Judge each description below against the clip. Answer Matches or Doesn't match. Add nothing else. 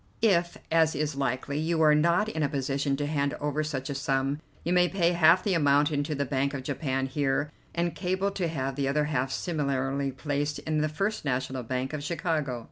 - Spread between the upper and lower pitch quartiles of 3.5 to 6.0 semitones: Doesn't match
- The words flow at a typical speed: Doesn't match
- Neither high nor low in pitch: Matches